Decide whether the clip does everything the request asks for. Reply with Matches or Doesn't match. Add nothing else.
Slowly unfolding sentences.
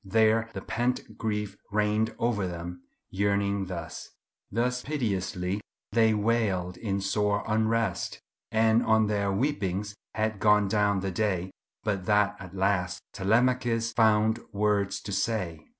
Matches